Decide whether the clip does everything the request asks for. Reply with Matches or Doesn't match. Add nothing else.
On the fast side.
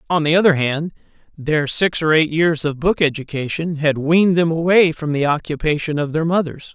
Doesn't match